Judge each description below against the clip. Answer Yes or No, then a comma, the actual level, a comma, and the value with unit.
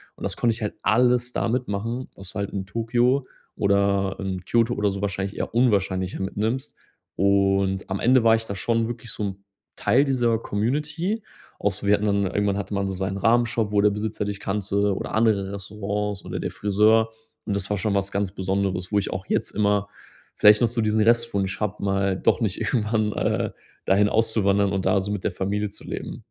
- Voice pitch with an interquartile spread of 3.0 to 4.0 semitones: No, narrow, 2.4 semitones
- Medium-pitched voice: No, low, 105 Hz